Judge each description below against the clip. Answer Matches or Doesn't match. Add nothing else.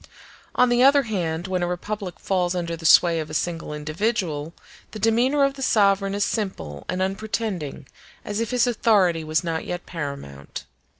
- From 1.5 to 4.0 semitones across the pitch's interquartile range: Doesn't match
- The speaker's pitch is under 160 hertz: Doesn't match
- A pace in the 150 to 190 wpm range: Matches